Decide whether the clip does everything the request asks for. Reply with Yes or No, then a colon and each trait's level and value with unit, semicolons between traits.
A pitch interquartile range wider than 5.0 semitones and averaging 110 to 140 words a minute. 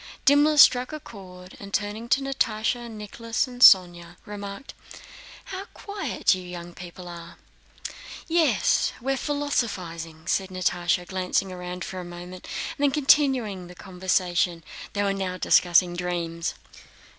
Yes: wide, 5.5 semitones; slow, 135 wpm